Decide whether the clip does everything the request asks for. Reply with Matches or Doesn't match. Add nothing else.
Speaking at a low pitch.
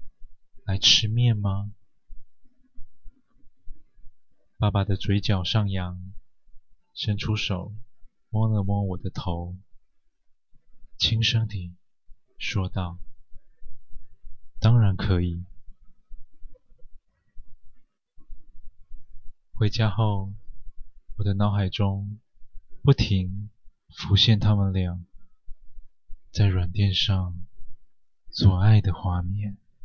Matches